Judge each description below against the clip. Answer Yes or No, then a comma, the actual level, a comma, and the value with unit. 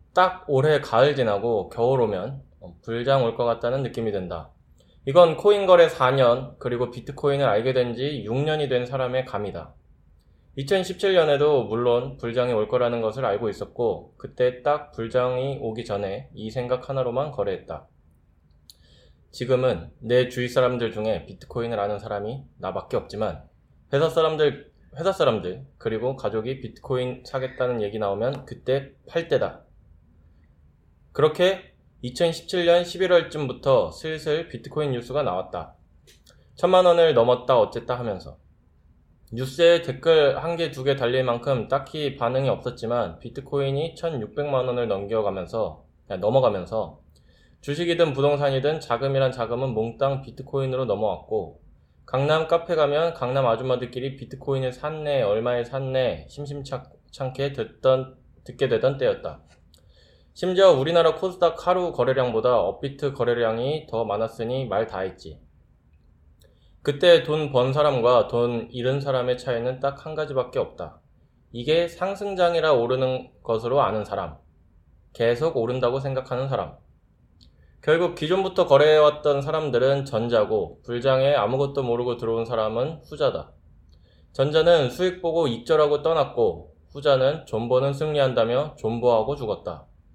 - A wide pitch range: No, average, 4.8 semitones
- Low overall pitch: Yes, low, 130 Hz